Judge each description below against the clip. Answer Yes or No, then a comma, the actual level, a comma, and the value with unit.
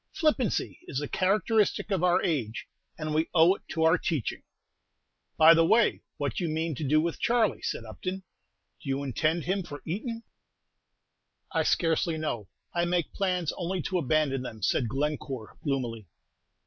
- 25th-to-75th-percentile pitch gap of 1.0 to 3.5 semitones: No, average, 4.4 semitones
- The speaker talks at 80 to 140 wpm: No, average, 165 wpm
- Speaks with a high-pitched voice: No, medium, 160 Hz